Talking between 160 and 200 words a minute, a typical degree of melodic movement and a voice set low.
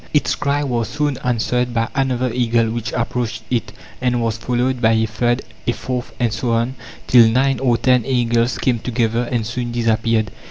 No: average, 185 wpm; narrow, 1.7 semitones; low, 120 Hz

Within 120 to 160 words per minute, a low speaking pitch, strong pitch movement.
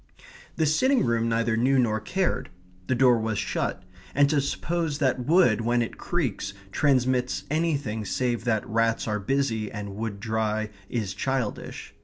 No: average, 155 wpm; low, 120 Hz; average, 4.1 semitones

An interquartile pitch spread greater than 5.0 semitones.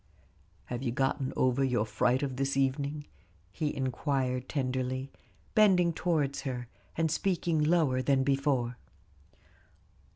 No: average, 2.7 semitones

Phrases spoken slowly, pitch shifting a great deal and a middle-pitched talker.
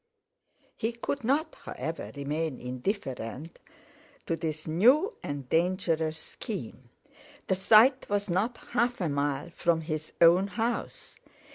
Yes: slow, 120 wpm; wide, 6.3 semitones; medium, 170 Hz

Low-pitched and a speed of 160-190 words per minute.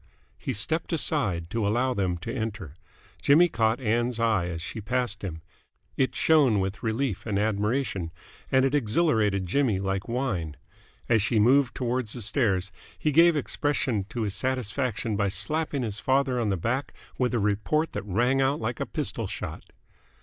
Yes: low, 115 Hz; average, 170 wpm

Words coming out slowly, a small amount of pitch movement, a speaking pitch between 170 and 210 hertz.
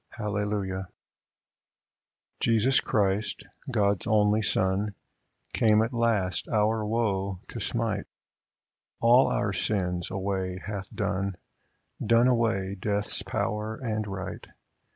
No: slow, 105 wpm; narrow, 2.3 semitones; low, 105 Hz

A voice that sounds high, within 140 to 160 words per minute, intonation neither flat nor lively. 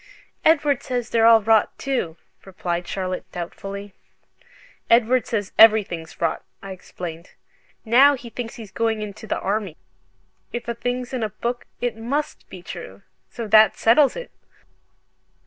Yes: high, 220 Hz; average, 145 wpm; average, 4.1 semitones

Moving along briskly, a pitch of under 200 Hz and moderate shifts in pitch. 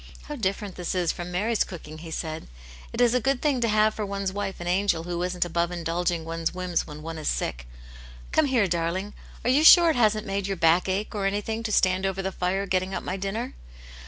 Yes: fast, 235 wpm; high, 190 Hz; average, 3.6 semitones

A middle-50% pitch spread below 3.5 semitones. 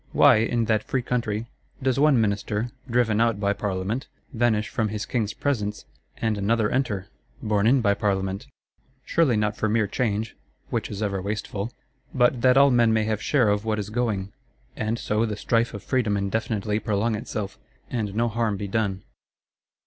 Yes: narrow, 2.4 semitones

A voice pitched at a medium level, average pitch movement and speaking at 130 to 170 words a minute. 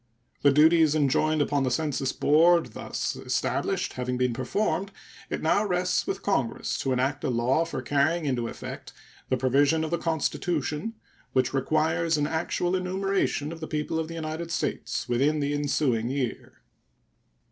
Yes: medium, 150 Hz; average, 3.7 semitones; average, 160 wpm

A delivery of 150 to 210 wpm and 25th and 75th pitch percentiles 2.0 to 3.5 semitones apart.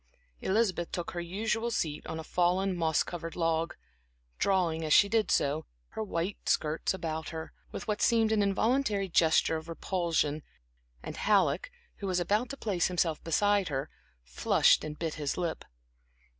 No: average, 160 wpm; average, 4.1 semitones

